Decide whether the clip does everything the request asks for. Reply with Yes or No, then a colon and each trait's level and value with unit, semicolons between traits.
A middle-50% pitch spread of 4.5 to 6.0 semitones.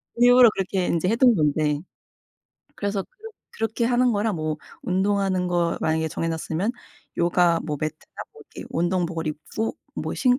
Yes: wide, 5.4 semitones